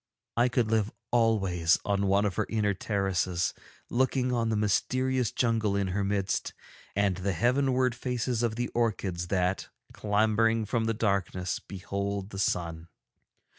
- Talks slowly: No, average, 145 wpm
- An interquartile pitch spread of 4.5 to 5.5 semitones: No, average, 3.2 semitones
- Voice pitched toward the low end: Yes, low, 105 Hz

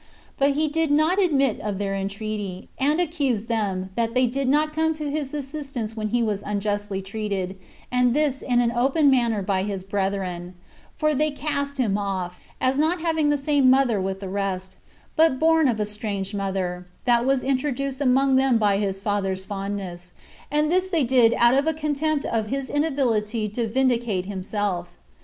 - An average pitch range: No, wide, 6.0 semitones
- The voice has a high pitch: Yes, high, 235 Hz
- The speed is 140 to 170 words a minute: No, average, 180 wpm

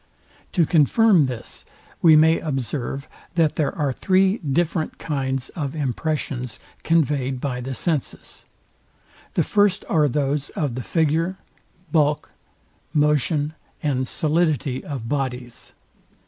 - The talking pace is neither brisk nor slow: No, slow, 115 wpm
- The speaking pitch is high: No, medium, 150 Hz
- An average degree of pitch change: Yes, average, 3.4 semitones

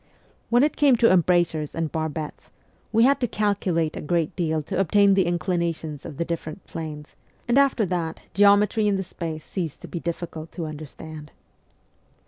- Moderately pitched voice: Yes, medium, 170 Hz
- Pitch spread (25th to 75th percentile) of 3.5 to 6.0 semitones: Yes, average, 4.2 semitones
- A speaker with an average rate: Yes, average, 175 wpm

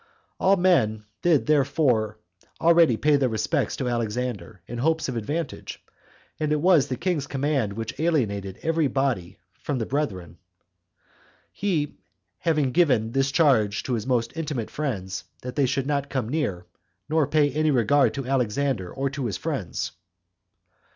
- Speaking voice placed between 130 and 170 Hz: Yes, low, 135 Hz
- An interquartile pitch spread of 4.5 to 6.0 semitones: Yes, average, 5.1 semitones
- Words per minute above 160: No, average, 150 wpm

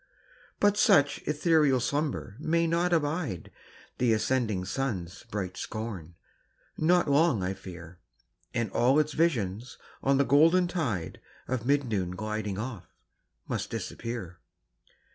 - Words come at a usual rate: No, slow, 125 wpm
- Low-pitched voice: Yes, low, 125 Hz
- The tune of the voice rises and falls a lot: Yes, wide, 7.5 semitones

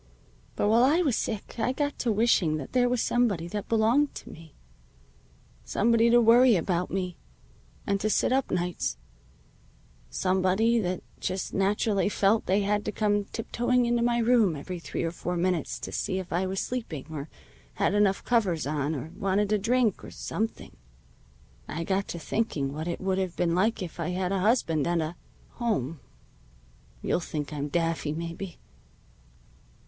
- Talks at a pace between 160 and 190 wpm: Yes, average, 170 wpm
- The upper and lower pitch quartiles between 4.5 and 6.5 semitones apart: Yes, average, 5.1 semitones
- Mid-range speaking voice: No, high, 195 Hz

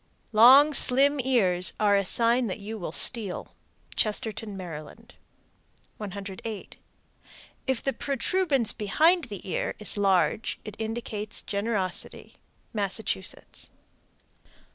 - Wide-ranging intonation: No, average, 3.6 semitones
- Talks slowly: Yes, slow, 100 wpm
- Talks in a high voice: Yes, high, 215 Hz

